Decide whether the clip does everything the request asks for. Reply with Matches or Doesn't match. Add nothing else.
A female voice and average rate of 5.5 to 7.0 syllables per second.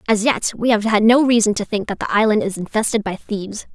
Matches